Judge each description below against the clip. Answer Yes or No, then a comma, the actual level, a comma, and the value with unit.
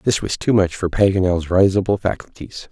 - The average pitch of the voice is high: No, very low, 95 Hz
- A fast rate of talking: No, average, 175 wpm